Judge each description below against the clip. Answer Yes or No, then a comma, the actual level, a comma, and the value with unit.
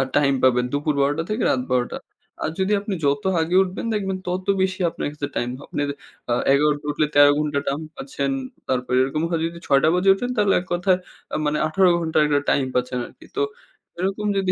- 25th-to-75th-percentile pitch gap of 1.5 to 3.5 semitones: No, average, 5.0 semitones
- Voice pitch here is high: No, medium, 155 Hz